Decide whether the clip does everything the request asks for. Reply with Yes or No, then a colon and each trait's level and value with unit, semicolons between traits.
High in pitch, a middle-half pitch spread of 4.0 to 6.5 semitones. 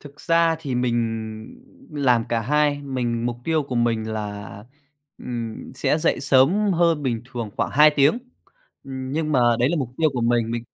No: low, 130 Hz; average, 4.3 semitones